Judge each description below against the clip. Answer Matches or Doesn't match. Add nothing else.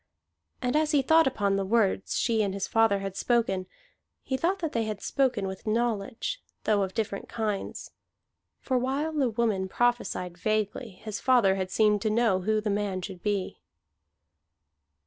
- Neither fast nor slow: Matches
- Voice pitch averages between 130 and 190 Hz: Doesn't match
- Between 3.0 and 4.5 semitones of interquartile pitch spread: Matches